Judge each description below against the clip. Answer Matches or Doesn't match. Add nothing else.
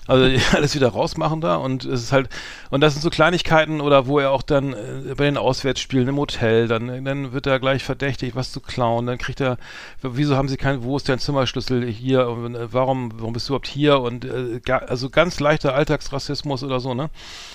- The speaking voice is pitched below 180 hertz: Matches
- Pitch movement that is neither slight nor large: Doesn't match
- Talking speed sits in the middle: Doesn't match